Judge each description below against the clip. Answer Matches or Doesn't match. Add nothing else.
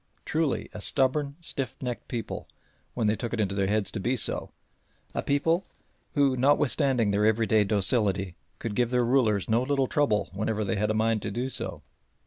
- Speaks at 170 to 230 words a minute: Matches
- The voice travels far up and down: Doesn't match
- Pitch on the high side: Doesn't match